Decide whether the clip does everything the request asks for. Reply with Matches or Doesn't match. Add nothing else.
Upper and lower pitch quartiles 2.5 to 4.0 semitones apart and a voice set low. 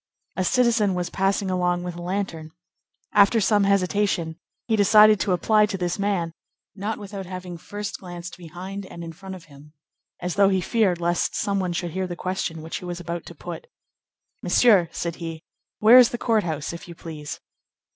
Doesn't match